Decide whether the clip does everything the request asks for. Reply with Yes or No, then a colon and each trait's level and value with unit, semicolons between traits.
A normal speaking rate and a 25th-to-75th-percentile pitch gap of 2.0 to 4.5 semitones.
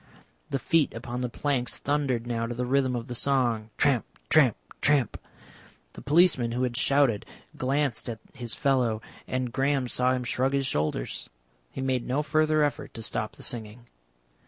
Yes: average, 170 wpm; average, 2.8 semitones